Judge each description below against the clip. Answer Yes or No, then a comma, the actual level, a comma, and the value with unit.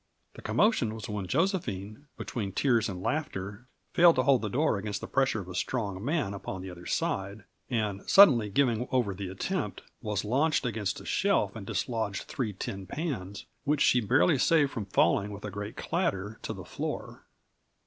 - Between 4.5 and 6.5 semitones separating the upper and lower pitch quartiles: Yes, wide, 5.4 semitones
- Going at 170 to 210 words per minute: Yes, average, 180 wpm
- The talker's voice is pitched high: No, low, 110 Hz